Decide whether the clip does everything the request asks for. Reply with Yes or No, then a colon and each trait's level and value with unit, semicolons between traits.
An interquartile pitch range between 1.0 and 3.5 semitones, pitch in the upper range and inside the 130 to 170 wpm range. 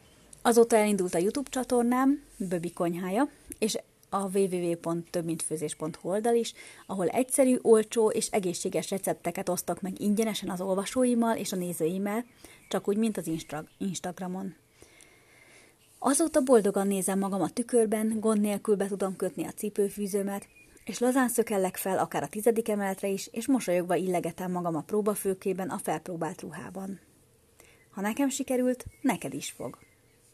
No: average, 4.2 semitones; high, 200 Hz; average, 135 wpm